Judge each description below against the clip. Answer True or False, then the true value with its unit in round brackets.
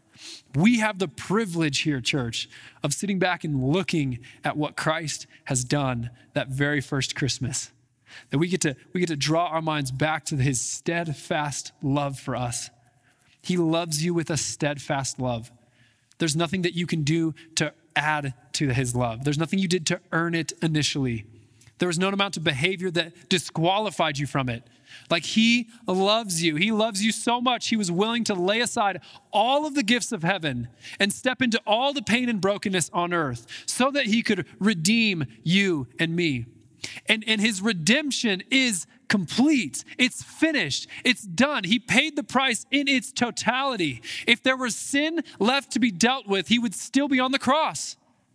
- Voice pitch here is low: False (170 Hz)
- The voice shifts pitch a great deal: True (7.6 semitones)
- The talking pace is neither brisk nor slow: True (180 wpm)